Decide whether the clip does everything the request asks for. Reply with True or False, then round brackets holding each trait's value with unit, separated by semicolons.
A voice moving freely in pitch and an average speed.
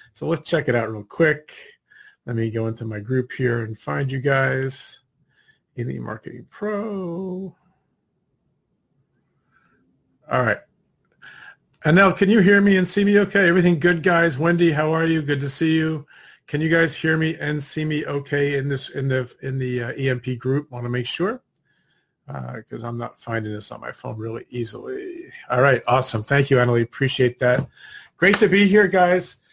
True (6.1 semitones; 185 wpm)